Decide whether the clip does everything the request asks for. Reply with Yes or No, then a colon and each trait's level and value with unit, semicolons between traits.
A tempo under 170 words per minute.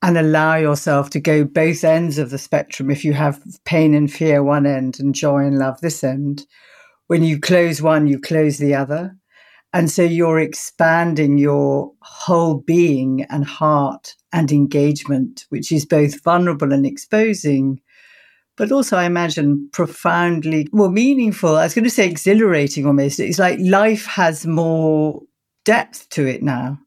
Yes: average, 160 wpm